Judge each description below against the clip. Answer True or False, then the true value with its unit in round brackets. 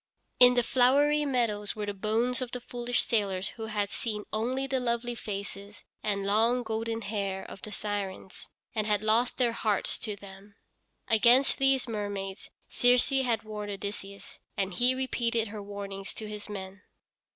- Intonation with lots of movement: False (3.2 semitones)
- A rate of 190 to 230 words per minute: False (165 wpm)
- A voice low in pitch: False (215 Hz)